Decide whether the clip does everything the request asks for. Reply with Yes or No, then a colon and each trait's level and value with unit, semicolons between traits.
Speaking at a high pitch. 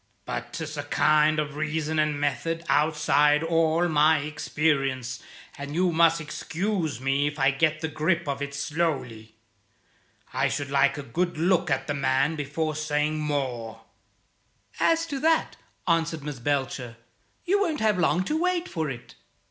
No: medium, 155 Hz